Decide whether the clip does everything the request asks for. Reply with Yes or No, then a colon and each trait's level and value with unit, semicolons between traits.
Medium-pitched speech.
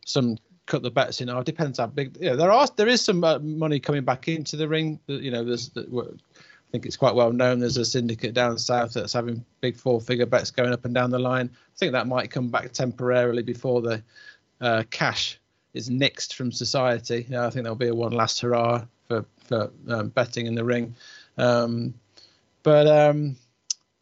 No: low, 125 Hz